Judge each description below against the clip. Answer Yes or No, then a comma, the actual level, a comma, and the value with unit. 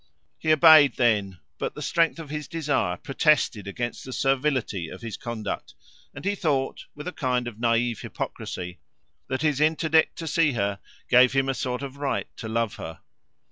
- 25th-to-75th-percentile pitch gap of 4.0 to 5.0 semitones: Yes, average, 4.6 semitones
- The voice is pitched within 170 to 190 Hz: No, low, 130 Hz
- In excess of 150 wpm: Yes, average, 180 wpm